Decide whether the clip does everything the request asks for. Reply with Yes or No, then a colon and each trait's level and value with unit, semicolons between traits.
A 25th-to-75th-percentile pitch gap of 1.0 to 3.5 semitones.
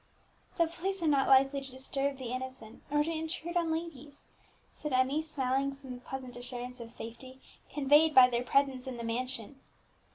Yes: average, 2.8 semitones